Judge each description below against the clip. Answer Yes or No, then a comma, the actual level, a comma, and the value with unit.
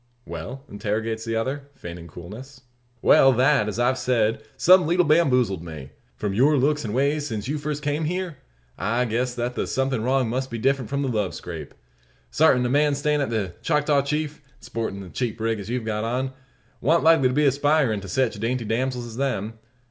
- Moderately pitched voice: No, low, 125 Hz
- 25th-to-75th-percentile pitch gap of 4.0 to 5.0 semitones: Yes, average, 4.3 semitones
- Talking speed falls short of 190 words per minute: No, average, 200 wpm